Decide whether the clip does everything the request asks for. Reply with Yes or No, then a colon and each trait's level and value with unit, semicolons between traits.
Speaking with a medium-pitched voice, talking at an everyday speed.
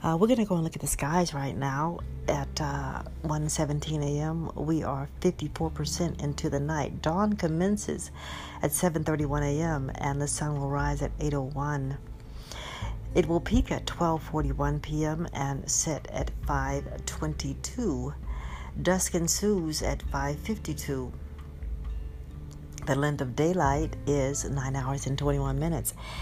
No: medium, 145 Hz; slow, 130 wpm